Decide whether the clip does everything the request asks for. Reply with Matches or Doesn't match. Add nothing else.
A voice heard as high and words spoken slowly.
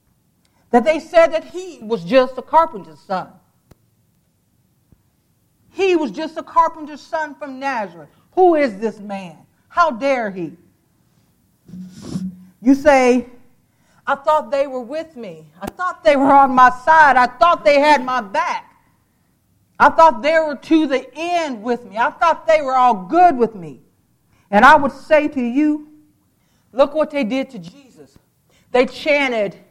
Doesn't match